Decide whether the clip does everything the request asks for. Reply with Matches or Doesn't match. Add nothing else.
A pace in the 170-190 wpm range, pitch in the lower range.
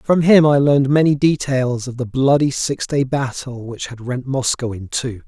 Doesn't match